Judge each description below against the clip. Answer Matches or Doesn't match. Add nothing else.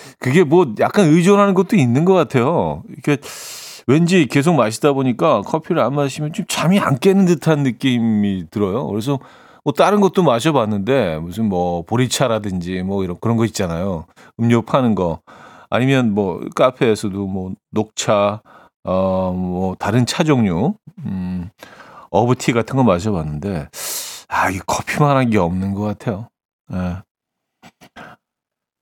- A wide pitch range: Matches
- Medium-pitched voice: Doesn't match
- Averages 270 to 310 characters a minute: Matches